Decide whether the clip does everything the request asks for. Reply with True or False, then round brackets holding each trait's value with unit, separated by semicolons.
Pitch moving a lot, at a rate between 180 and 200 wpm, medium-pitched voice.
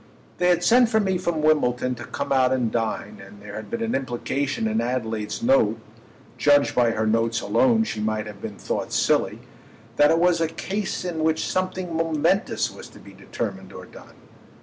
True (7.8 semitones; 185 wpm; 145 Hz)